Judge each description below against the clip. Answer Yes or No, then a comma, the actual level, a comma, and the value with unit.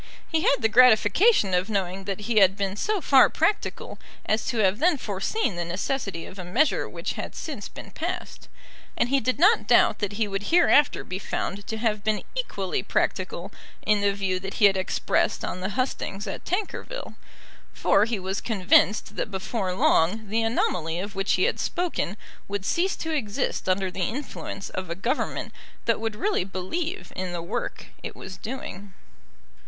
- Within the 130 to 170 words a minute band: No, average, 180 wpm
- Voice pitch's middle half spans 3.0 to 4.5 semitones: No, average, 5.0 semitones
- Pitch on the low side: No, high, 205 Hz